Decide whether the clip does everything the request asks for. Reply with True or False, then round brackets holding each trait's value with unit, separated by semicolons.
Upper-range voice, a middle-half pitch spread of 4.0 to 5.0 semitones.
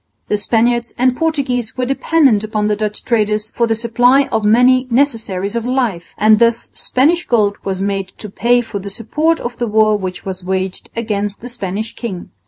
False (225 Hz; 3.2 semitones)